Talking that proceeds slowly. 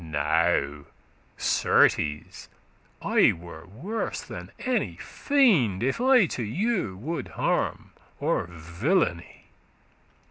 Yes: slow, 95 wpm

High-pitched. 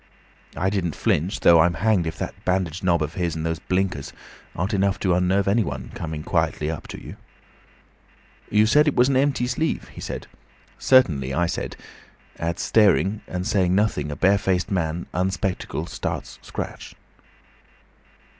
No: very low, 90 Hz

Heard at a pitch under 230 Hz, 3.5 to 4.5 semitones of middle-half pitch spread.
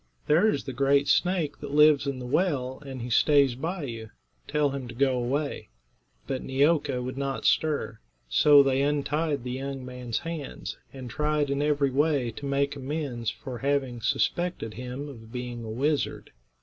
No: medium, 140 Hz; average, 2.7 semitones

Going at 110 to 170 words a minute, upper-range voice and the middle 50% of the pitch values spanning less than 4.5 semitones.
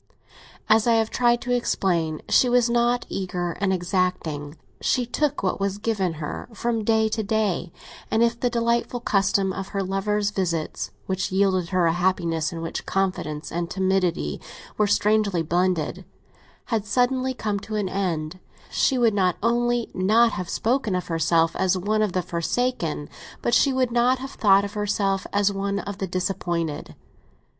Yes: average, 165 wpm; high, 195 Hz; average, 4.1 semitones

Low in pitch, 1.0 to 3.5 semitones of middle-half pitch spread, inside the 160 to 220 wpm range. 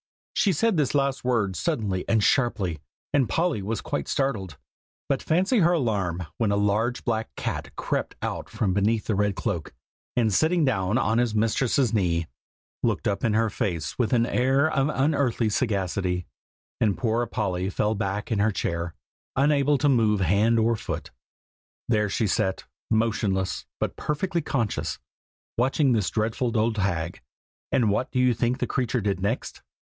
No: low, 110 Hz; average, 4.4 semitones; average, 165 wpm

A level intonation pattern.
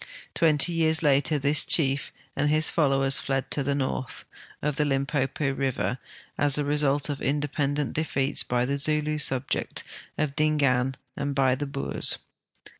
Yes: narrow, 1.7 semitones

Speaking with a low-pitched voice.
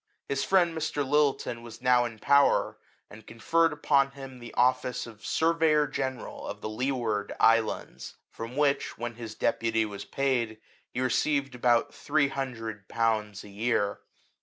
Yes: low, 125 Hz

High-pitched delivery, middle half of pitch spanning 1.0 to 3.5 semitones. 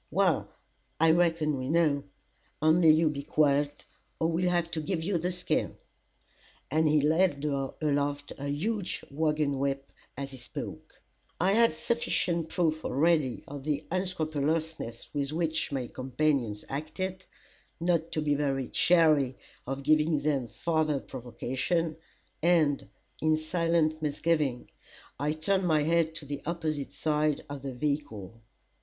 No: medium, 155 Hz; average, 2.8 semitones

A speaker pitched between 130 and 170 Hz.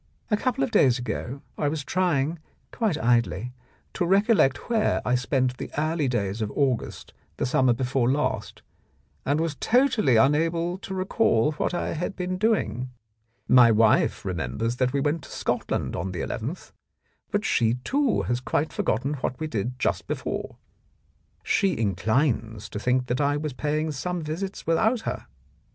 Yes: medium, 140 Hz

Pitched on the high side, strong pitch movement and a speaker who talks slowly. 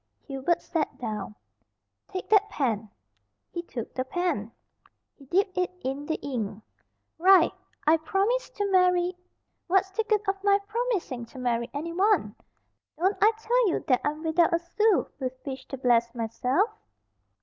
No: very high, 335 Hz; wide, 7.2 semitones; average, 155 wpm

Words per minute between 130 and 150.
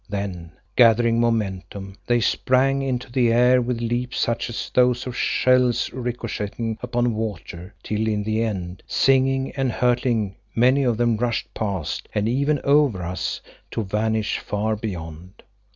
Yes: average, 145 wpm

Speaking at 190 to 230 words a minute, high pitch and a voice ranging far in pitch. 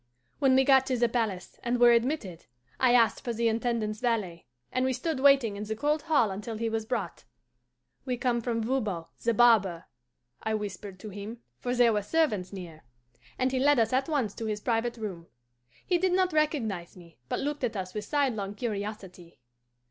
No: average, 195 wpm; high, 230 Hz; average, 3.9 semitones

